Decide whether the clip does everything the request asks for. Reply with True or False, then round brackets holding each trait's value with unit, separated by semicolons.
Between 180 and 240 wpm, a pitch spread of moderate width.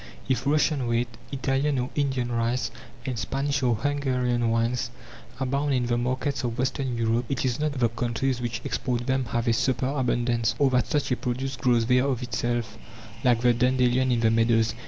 False (185 wpm; 2.1 semitones)